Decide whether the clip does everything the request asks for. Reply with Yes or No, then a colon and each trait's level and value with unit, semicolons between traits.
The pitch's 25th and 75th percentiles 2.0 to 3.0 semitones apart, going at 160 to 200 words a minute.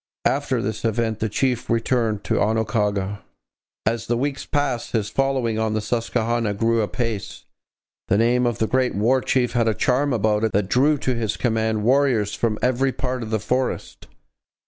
Yes: narrow, 2.6 semitones; average, 175 wpm